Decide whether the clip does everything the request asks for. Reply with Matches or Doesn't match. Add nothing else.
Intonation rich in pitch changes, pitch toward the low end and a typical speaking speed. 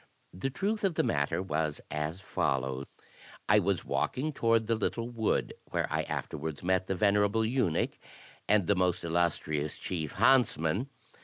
Matches